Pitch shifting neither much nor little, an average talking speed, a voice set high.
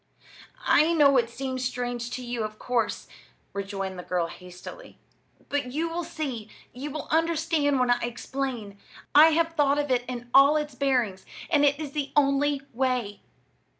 Yes: average, 3.6 semitones; average, 165 wpm; very high, 265 Hz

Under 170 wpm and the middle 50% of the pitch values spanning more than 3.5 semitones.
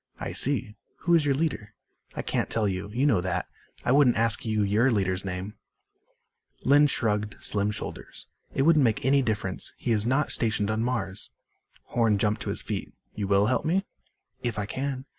No: average, 185 wpm; average, 4.4 semitones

